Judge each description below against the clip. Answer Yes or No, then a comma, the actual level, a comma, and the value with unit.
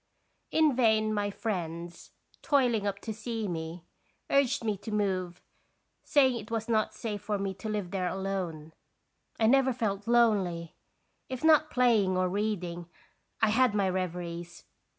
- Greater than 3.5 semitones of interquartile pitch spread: Yes, average, 4.1 semitones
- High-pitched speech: Yes, high, 210 Hz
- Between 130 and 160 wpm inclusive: Yes, average, 150 wpm